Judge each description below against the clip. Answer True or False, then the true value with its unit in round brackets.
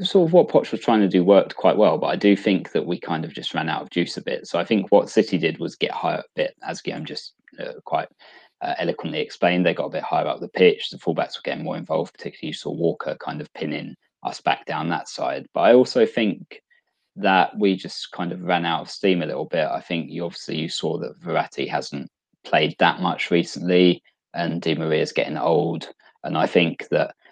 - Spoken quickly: True (240 wpm)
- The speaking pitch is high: False (100 Hz)